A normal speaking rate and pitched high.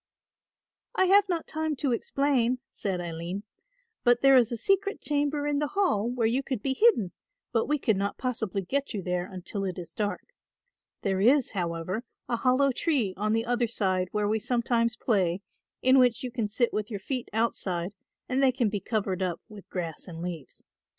Yes: average, 190 wpm; high, 230 Hz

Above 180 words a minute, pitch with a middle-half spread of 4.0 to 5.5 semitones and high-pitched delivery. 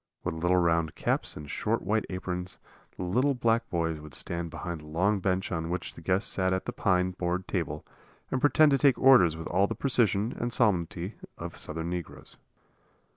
No: average, 190 wpm; average, 4.4 semitones; very low, 90 Hz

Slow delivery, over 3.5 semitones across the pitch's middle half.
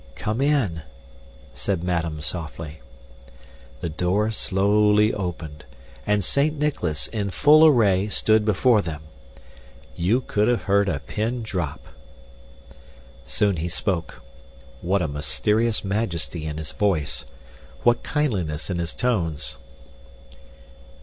Yes: slow, 115 wpm; average, 4.9 semitones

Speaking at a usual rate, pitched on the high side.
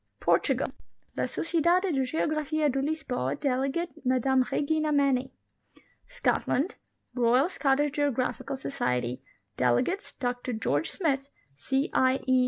No: slow, 110 wpm; very high, 270 Hz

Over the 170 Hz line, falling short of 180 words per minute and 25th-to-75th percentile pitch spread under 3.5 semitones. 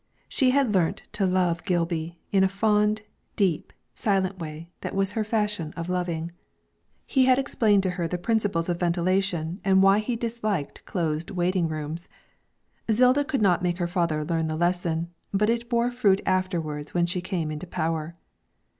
No: medium, 185 Hz; average, 170 wpm; average, 3.8 semitones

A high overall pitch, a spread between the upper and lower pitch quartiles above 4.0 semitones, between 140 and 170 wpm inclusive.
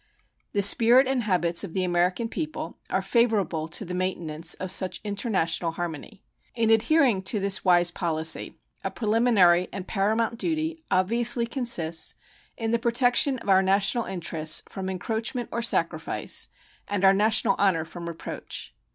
Yes: high, 195 Hz; average, 5.0 semitones; average, 150 wpm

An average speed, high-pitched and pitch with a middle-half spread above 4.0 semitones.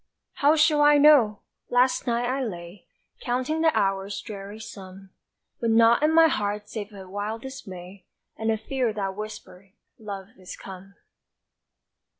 Yes: average, 150 wpm; high, 215 Hz; average, 4.7 semitones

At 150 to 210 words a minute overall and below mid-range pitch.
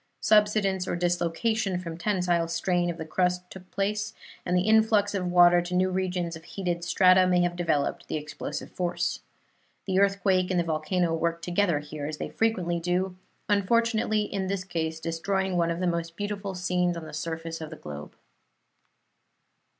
No: average, 175 wpm; medium, 180 Hz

